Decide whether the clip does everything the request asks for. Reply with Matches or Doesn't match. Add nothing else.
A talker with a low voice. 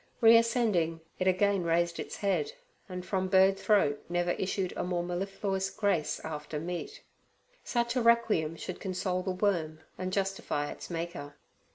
Doesn't match